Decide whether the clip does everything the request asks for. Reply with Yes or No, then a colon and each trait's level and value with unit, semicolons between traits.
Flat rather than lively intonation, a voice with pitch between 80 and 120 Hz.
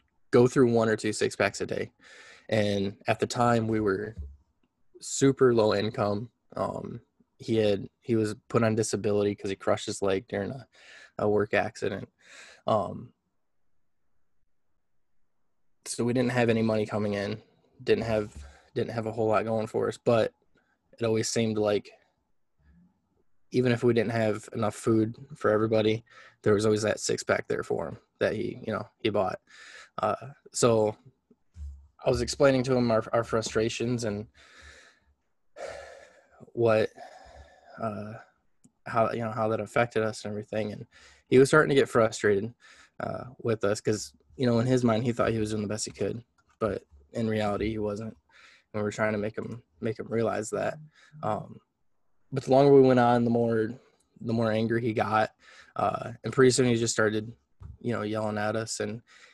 Yes: narrow, 2.0 semitones; low, 110 Hz